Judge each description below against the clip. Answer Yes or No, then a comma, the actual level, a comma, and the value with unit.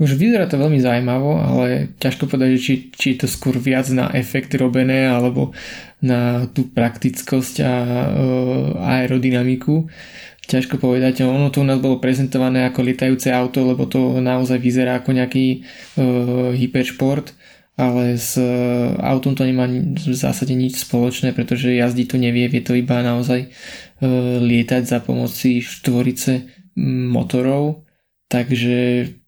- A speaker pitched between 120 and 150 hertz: Yes, low, 130 Hz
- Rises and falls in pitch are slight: Yes, narrow, 1.0 semitones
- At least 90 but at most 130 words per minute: No, average, 140 wpm